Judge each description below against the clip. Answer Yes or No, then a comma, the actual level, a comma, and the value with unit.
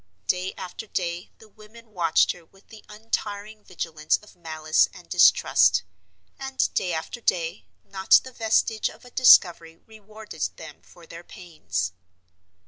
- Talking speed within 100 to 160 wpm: Yes, average, 140 wpm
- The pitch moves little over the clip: No, average, 4.8 semitones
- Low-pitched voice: No, medium, 185 Hz